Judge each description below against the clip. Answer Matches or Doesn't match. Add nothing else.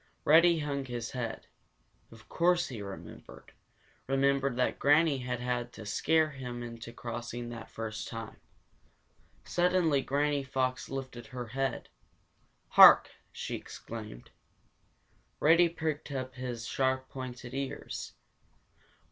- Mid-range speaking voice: Doesn't match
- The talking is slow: Matches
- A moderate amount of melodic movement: Matches